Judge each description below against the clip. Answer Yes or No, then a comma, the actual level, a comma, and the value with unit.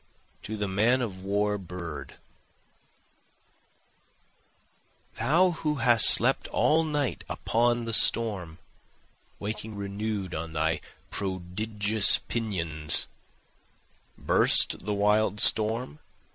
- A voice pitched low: Yes, low, 105 Hz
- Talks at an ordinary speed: No, slow, 90 wpm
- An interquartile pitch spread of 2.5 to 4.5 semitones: Yes, average, 3.6 semitones